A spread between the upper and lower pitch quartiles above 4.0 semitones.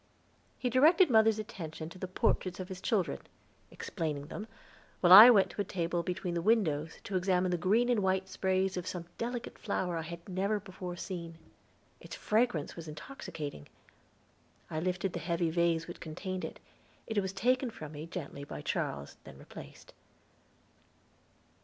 No: average, 3.6 semitones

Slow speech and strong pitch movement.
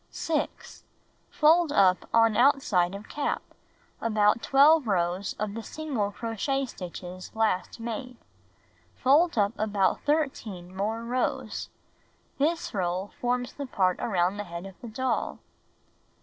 Yes: slow, 125 wpm; wide, 5.8 semitones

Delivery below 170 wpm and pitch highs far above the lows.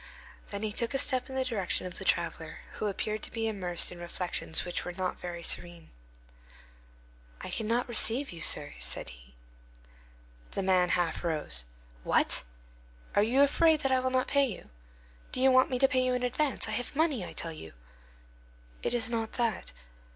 No: average, 190 wpm; wide, 6.5 semitones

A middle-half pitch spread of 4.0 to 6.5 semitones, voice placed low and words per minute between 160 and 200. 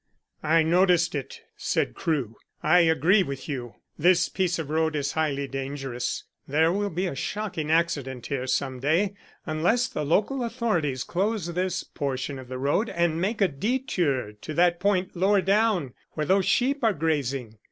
No: wide, 5.4 semitones; medium, 160 Hz; average, 165 wpm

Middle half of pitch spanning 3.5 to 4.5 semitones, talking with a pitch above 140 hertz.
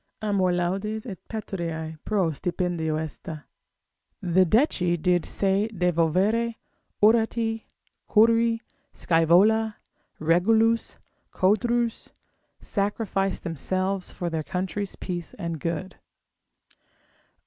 Yes: average, 4.2 semitones; high, 190 Hz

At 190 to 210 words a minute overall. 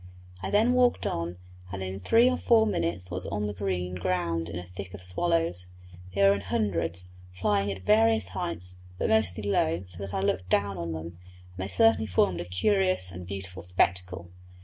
Yes: average, 195 wpm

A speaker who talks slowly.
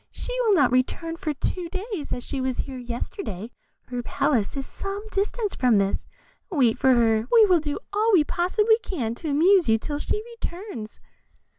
No: average, 180 wpm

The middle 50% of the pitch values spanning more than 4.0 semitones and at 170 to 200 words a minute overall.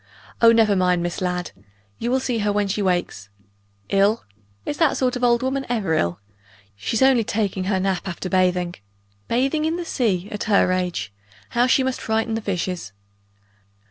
Yes: average, 5.0 semitones; average, 175 wpm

